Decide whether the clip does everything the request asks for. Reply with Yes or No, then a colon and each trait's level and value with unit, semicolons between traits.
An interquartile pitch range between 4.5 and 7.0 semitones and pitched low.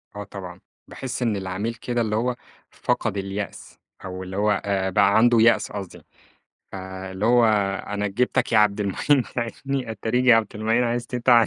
No: average, 3.4 semitones; low, 105 Hz